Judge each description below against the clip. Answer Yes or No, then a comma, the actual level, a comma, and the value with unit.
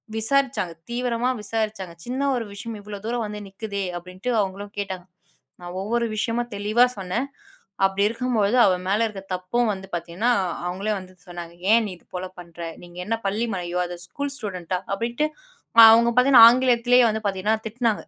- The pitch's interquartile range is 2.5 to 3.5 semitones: No, average, 4.0 semitones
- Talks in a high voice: Yes, high, 210 Hz